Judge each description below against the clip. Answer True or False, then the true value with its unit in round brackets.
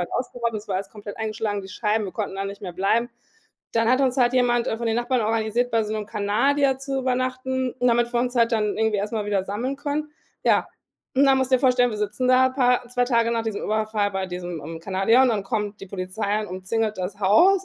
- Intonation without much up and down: False (3.5 semitones)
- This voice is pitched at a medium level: False (225 Hz)